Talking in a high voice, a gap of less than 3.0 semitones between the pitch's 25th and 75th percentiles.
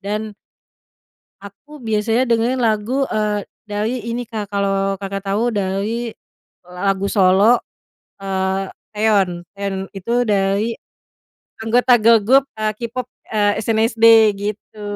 Yes: high, 210 Hz; narrow, 2.6 semitones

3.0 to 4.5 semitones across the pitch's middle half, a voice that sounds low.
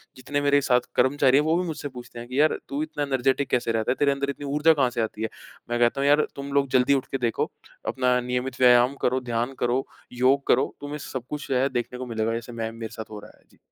No: narrow, 2.6 semitones; low, 130 Hz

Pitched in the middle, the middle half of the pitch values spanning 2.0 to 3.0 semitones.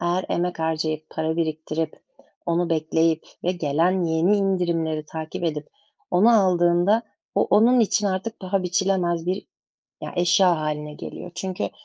Yes: medium, 175 Hz; average, 2.7 semitones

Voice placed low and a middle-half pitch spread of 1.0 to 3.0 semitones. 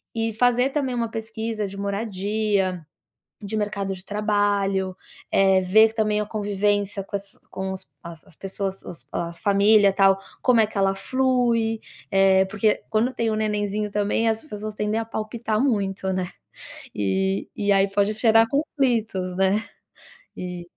No: high, 205 Hz; narrow, 2.4 semitones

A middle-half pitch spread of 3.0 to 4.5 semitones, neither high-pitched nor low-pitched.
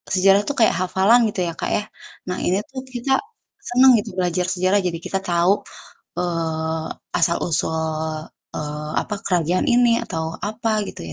Yes: average, 4.2 semitones; medium, 180 Hz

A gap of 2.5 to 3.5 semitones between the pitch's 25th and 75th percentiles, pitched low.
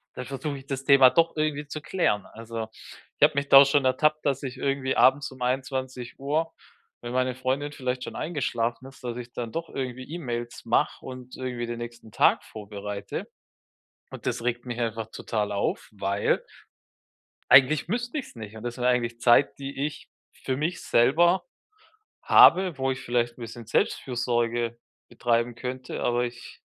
Yes: average, 2.8 semitones; low, 130 Hz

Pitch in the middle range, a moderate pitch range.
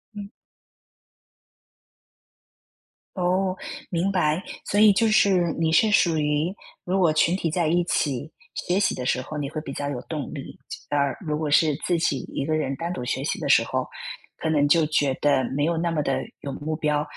Yes: medium, 160 Hz; average, 3.3 semitones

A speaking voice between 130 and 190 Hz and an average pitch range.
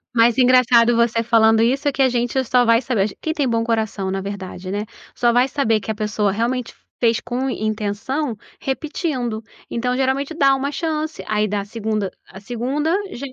No: high, 235 Hz; average, 3.5 semitones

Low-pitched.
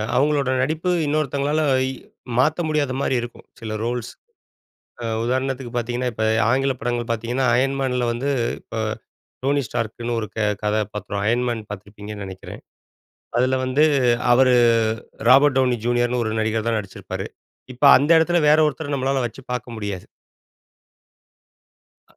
Yes: low, 125 Hz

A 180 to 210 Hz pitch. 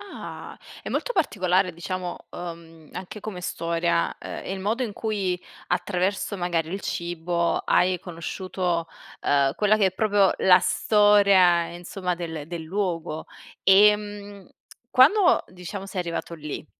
Yes: medium, 185 Hz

